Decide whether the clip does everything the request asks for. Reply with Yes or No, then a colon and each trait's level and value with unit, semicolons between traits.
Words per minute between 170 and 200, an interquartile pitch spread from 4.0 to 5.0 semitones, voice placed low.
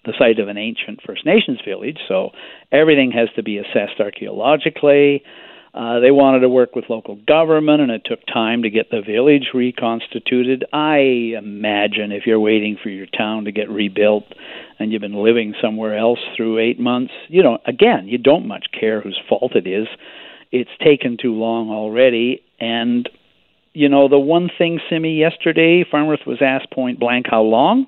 Yes: average, 180 wpm; average, 4.3 semitones; low, 120 Hz